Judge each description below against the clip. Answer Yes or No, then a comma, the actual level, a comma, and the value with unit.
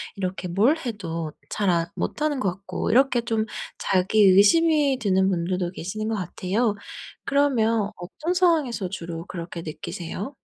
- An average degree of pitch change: No, wide, 5.7 semitones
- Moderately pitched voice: No, high, 200 Hz